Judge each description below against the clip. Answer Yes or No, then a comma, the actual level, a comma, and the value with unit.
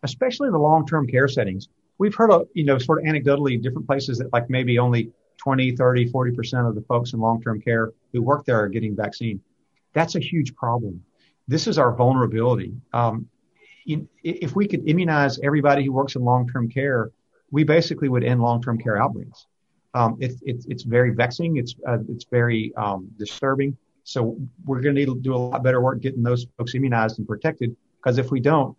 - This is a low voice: Yes, low, 125 Hz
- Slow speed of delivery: No, average, 200 wpm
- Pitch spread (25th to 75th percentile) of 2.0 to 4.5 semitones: Yes, average, 3.0 semitones